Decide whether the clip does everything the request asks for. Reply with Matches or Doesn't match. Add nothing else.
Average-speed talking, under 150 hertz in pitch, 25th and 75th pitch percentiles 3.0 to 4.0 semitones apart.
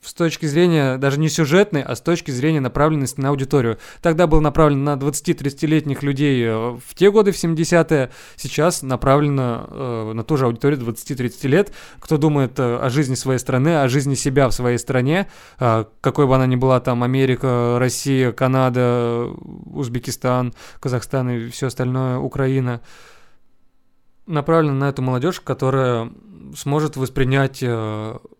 Matches